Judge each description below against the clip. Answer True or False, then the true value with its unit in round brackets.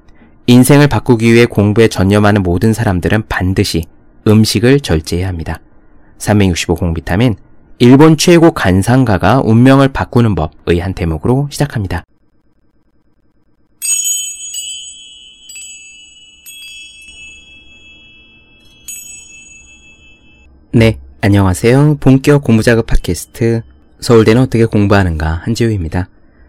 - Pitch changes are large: True (6.2 semitones)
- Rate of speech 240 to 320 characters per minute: False (220 characters per minute)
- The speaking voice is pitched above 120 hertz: False (105 Hz)